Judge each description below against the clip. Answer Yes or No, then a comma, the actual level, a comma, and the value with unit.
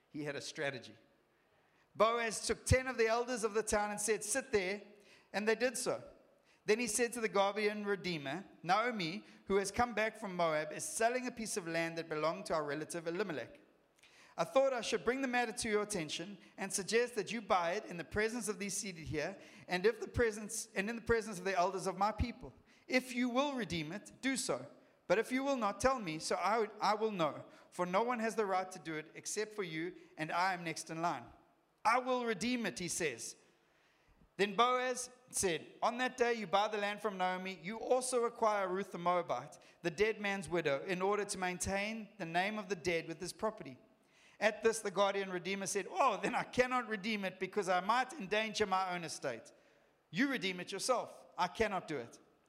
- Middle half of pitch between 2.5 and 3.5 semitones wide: No, average, 3.9 semitones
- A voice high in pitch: Yes, high, 205 Hz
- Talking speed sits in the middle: No, fast, 215 wpm